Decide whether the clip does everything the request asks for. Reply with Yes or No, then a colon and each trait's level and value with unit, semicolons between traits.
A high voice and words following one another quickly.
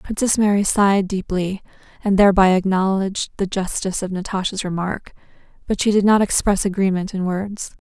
No: high, 195 Hz; average, 155 wpm